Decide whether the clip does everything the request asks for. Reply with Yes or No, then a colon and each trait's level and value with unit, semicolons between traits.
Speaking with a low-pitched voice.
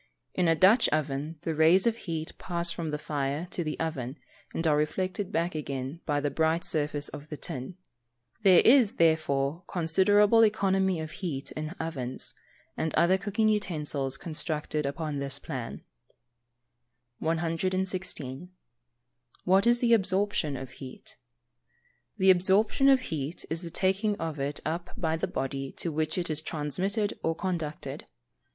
No: medium, 165 Hz